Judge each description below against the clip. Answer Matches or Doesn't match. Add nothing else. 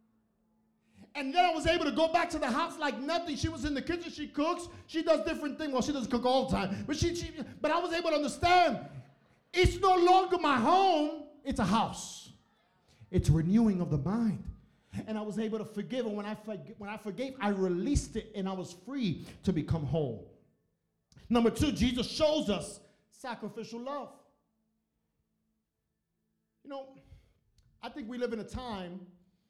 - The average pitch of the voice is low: Doesn't match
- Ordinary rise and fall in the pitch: Doesn't match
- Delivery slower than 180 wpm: Doesn't match